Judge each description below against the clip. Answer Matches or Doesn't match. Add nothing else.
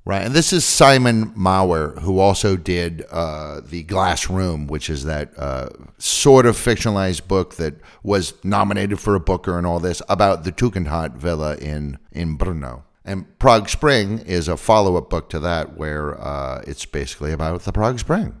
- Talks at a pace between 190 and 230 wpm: Doesn't match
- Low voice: Matches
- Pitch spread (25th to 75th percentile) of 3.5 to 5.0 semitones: Matches